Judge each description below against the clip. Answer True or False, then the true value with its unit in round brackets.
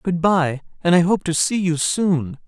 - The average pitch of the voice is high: False (170 Hz)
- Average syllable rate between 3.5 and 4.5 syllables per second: True (4.2 syllables/s)